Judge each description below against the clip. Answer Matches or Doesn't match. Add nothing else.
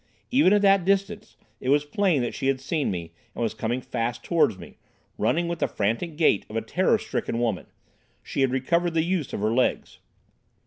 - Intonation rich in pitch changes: Matches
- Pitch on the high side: Doesn't match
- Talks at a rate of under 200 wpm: Doesn't match